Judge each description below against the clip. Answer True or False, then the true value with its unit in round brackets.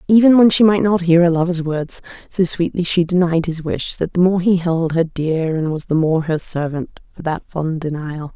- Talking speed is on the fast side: True (230 wpm)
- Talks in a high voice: False (170 Hz)